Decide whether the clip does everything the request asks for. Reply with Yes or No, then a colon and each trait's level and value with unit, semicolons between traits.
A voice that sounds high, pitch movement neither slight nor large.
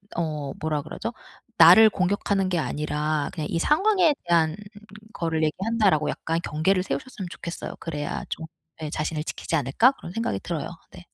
No: medium, 165 Hz; average, 4.2 semitones